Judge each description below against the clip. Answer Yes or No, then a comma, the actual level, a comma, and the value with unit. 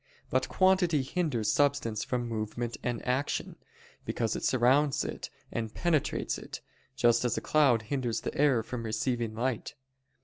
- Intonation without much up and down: No, average, 3.7 semitones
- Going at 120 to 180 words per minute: Yes, average, 145 wpm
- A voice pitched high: No, low, 125 Hz